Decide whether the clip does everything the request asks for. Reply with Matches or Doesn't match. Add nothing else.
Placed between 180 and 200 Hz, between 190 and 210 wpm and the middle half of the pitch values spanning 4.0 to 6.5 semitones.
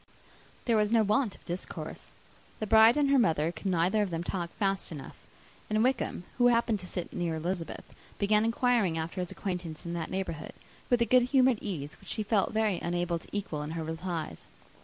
Matches